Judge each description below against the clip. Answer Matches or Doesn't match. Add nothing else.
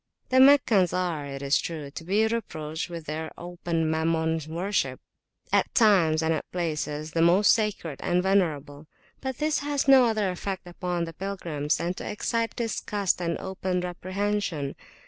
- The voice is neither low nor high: Matches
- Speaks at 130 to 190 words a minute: Matches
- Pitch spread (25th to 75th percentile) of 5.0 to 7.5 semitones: Doesn't match